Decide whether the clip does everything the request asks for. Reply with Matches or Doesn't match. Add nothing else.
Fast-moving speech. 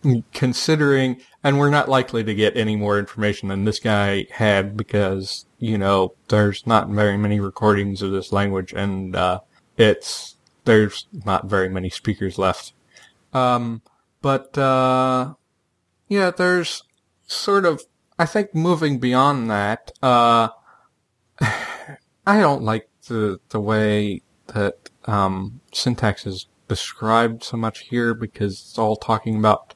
Doesn't match